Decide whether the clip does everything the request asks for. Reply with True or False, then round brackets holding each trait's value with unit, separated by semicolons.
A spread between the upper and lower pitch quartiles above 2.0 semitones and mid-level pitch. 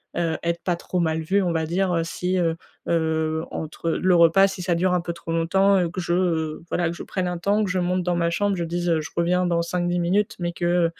False (1.5 semitones; 175 Hz)